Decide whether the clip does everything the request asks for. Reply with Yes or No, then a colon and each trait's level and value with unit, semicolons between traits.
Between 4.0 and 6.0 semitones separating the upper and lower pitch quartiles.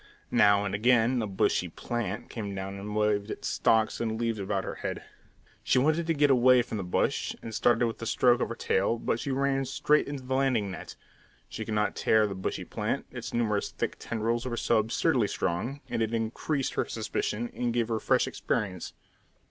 No: average, 3.1 semitones